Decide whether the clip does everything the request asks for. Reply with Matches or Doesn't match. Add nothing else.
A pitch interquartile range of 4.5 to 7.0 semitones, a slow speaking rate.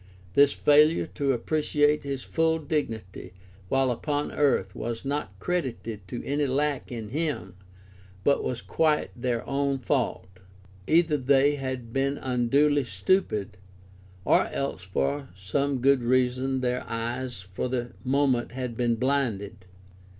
Doesn't match